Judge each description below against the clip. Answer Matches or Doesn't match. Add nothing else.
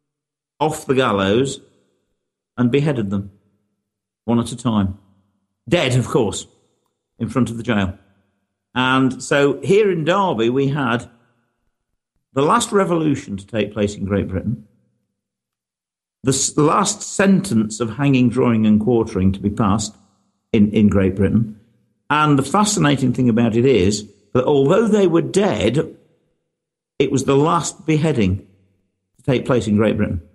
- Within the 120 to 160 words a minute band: Matches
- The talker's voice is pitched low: Matches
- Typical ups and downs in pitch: Doesn't match